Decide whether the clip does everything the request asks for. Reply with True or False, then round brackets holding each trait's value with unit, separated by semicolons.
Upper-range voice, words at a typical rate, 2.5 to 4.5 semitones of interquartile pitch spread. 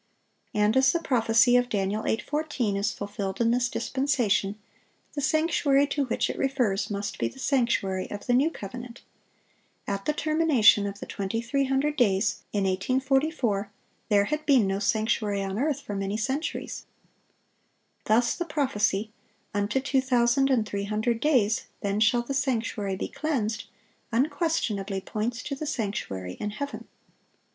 False (230 Hz; 150 wpm; 5.0 semitones)